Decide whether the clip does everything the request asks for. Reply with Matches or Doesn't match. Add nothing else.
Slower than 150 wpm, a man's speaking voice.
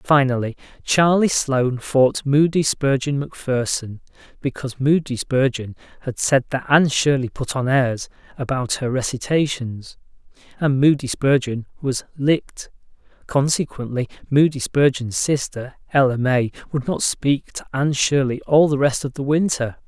Matches